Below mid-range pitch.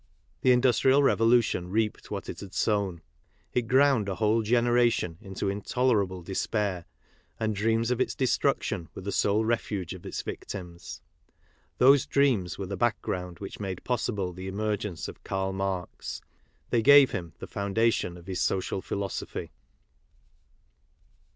Yes: low, 105 Hz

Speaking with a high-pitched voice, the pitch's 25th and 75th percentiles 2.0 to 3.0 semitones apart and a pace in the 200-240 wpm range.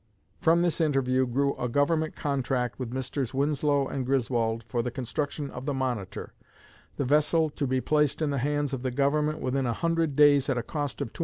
No: medium, 140 Hz; average, 2.7 semitones; fast, 205 wpm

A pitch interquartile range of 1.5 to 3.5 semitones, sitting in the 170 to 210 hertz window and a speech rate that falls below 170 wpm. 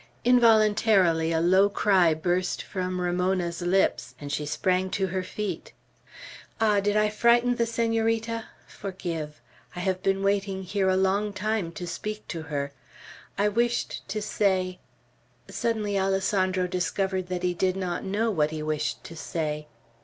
Yes: average, 3.0 semitones; high, 190 Hz; average, 155 wpm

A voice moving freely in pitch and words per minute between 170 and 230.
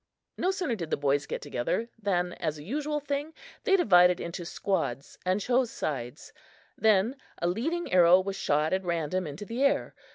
Yes: wide, 6.9 semitones; average, 175 wpm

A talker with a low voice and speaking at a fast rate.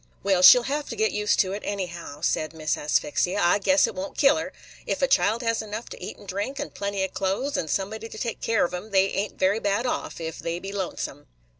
No: high, 200 Hz; fast, 250 wpm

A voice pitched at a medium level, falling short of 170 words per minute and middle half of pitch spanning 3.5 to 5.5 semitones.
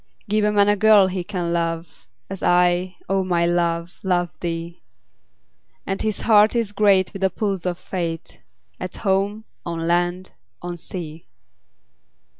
No: medium, 180 Hz; average, 155 wpm; narrow, 2.5 semitones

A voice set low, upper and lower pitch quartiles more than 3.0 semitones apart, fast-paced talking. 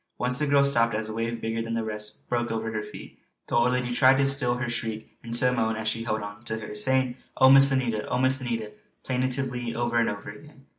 No: low, 120 Hz; narrow, 2.6 semitones; fast, 245 wpm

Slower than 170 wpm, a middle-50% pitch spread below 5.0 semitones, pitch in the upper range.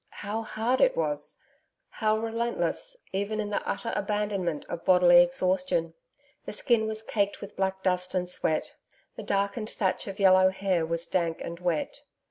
Yes: average, 160 wpm; average, 3.2 semitones; high, 195 Hz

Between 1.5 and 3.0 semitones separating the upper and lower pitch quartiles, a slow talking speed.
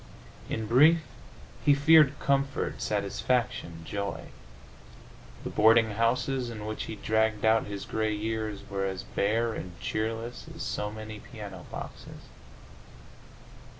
Yes: narrow, 2.4 semitones; slow, 120 wpm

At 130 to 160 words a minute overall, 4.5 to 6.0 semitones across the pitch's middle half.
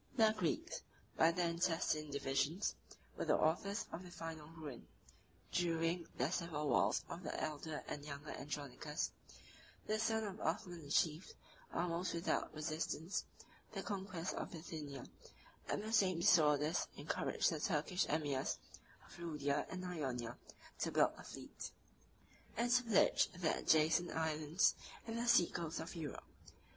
No: average, 145 wpm; average, 3.1 semitones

